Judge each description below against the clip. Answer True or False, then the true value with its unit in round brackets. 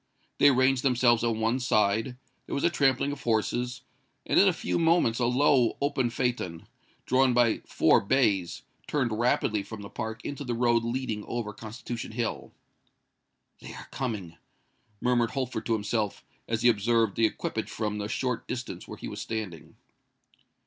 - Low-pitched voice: True (120 Hz)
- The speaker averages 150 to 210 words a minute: True (165 wpm)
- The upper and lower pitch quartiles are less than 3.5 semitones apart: True (2.8 semitones)